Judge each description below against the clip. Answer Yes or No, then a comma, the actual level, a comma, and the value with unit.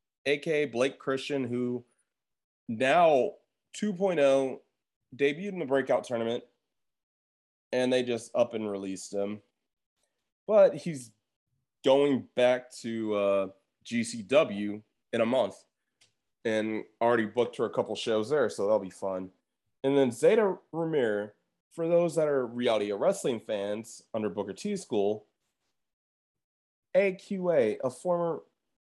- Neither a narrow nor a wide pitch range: No, wide, 5.8 semitones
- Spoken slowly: Yes, slow, 120 wpm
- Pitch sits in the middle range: No, low, 125 Hz